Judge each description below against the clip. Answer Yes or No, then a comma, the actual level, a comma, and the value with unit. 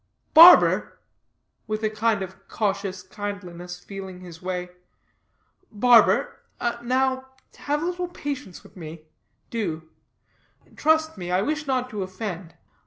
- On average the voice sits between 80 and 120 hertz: No, high, 205 Hz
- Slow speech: Yes, slow, 120 wpm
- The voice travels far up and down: Yes, wide, 6.2 semitones